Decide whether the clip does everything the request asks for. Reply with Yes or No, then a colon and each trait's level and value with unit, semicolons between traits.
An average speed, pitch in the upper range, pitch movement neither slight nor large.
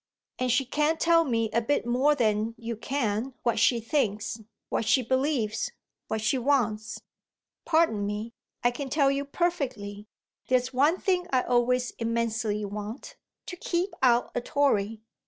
Yes: average, 155 wpm; high, 245 Hz; average, 4.3 semitones